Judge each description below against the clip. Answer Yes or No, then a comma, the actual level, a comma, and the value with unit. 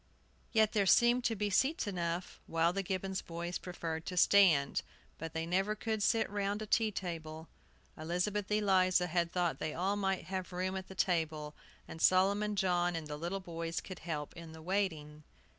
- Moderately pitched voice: Yes, medium, 180 Hz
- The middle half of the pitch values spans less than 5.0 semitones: Yes, average, 3.2 semitones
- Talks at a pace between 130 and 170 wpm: No, average, 180 wpm